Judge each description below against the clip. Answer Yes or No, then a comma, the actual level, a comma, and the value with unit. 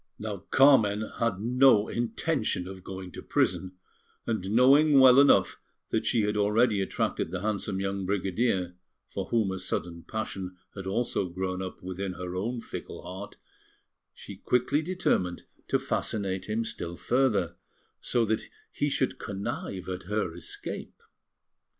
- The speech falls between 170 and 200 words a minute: No, average, 145 wpm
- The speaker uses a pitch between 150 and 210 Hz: No, low, 100 Hz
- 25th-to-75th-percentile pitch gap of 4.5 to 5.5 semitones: No, average, 4.1 semitones